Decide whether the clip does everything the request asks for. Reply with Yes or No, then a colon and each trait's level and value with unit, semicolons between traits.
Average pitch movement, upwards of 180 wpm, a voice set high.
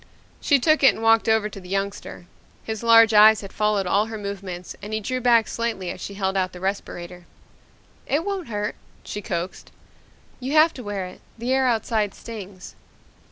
Yes: average, 3.1 semitones; average, 190 wpm; high, 210 Hz